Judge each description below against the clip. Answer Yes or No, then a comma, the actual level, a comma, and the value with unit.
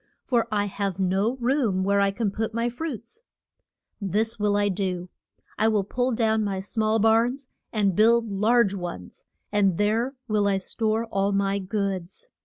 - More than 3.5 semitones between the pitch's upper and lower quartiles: No, narrow, 2.6 semitones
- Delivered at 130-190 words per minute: Yes, average, 165 wpm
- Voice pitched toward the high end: Yes, high, 210 Hz